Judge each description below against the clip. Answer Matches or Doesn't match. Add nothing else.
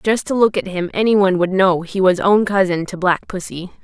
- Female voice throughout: Matches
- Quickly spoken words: Matches